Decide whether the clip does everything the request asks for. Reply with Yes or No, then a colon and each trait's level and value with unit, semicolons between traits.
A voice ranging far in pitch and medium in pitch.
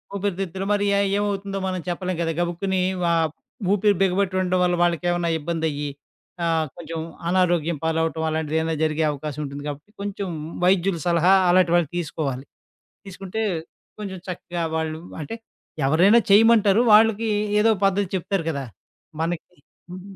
No: average, 3.3 semitones; medium, 175 Hz